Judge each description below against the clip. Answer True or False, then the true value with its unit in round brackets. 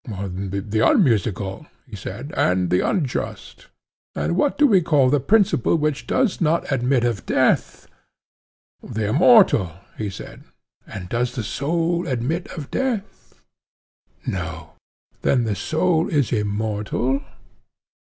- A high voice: False (125 Hz)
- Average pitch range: False (7.7 semitones)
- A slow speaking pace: True (125 wpm)